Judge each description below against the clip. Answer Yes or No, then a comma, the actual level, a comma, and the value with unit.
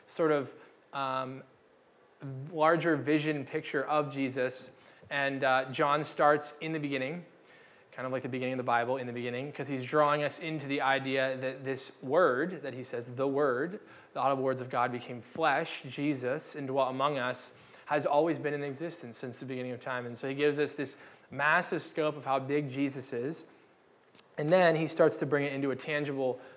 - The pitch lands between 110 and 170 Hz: Yes, medium, 140 Hz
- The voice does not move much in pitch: Yes, narrow, 2.2 semitones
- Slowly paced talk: No, average, 195 wpm